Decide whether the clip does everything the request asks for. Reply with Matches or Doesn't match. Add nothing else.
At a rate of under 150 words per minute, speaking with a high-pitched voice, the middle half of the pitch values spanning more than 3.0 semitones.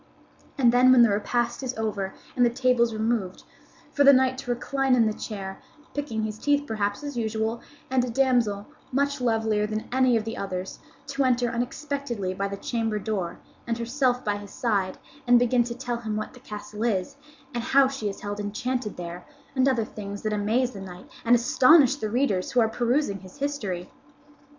Doesn't match